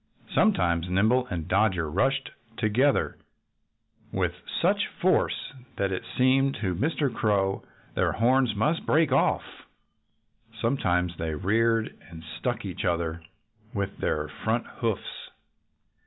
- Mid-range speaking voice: No, low, 110 Hz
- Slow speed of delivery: Yes, slow, 115 wpm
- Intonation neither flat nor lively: No, wide, 6.4 semitones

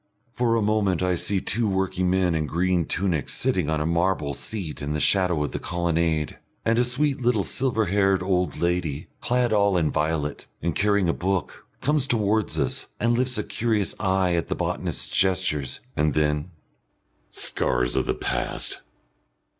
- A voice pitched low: Yes, very low, 90 Hz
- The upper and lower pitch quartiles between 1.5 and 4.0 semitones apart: No, average, 4.7 semitones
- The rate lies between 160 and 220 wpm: Yes, average, 170 wpm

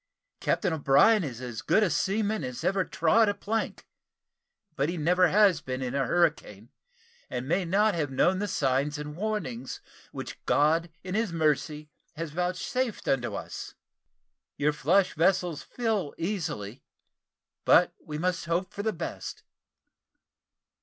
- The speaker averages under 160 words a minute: Yes, average, 145 wpm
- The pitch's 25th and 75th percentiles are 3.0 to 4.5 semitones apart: No, average, 5.1 semitones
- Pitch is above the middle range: No, medium, 165 Hz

